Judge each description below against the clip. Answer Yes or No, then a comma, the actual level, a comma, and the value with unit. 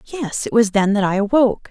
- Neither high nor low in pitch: No, high, 220 Hz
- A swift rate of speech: Yes, fast, 245 wpm